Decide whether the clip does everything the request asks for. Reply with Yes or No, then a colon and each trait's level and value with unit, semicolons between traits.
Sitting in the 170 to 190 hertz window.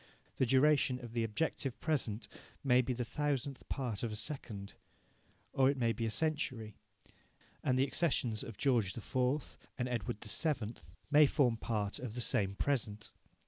No: low, 125 Hz